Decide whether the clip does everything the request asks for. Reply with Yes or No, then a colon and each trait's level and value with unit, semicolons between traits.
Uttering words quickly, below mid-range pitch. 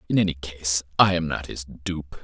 Yes: fast, 215 wpm; very low, 80 Hz